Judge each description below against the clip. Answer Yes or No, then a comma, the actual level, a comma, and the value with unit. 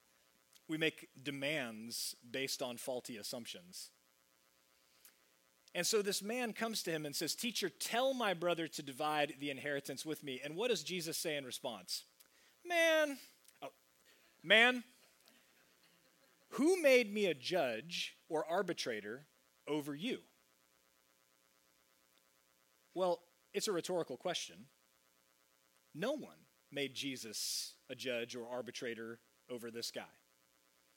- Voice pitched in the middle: No, low, 130 Hz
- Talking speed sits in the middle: No, slow, 120 wpm